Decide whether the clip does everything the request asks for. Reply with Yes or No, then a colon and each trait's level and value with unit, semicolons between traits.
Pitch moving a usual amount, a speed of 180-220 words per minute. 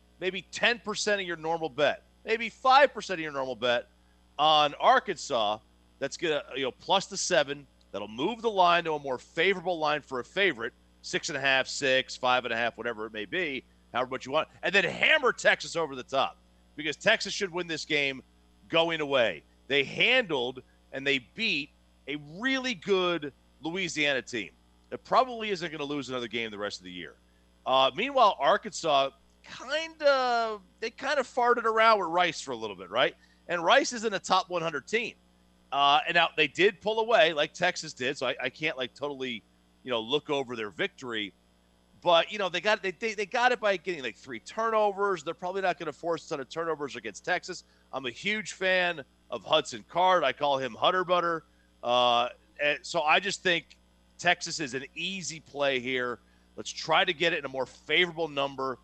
No: wide, 7.4 semitones; average, 200 wpm